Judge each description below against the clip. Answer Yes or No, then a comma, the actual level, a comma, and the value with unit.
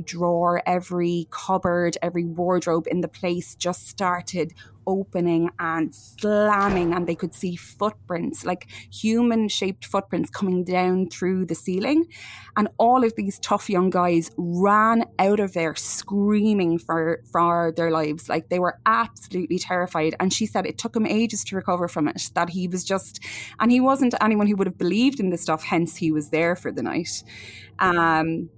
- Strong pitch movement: No, average, 3.2 semitones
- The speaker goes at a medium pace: Yes, average, 170 wpm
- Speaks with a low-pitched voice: No, medium, 180 Hz